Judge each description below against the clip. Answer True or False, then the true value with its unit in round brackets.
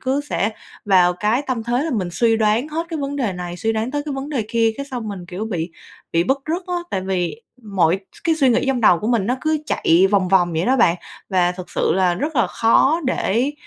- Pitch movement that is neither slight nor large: False (6.5 semitones)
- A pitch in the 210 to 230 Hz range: True (225 Hz)